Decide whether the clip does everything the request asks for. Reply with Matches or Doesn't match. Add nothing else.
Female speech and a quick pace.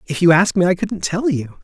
Doesn't match